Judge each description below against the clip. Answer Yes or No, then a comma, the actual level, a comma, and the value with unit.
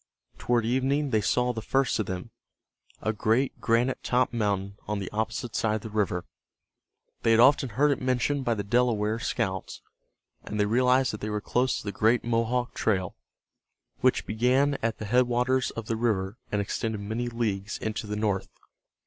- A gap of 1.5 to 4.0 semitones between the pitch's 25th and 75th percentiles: Yes, average, 2.9 semitones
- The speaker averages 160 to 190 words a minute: Yes, average, 180 wpm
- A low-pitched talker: Yes, low, 115 Hz